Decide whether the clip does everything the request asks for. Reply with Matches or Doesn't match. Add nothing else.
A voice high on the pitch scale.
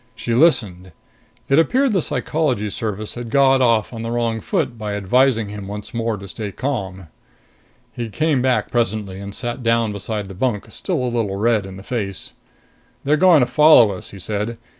Doesn't match